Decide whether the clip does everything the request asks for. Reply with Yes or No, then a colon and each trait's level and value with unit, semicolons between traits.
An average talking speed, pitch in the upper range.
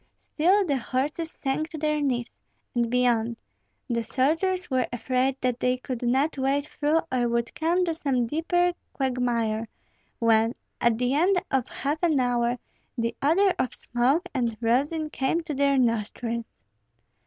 Yes: average, 155 wpm; very high, 260 Hz